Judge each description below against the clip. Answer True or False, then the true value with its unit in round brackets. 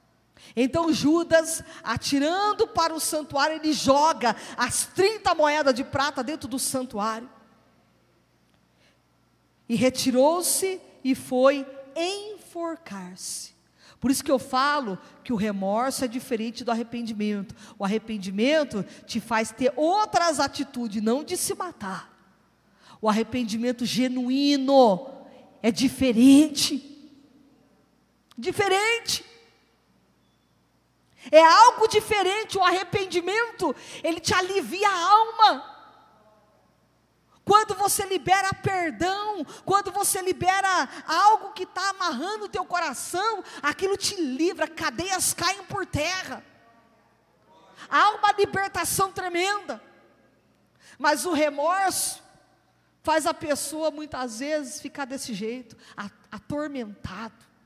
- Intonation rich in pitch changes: True (6.5 semitones)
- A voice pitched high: True (300 Hz)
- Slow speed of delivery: True (100 wpm)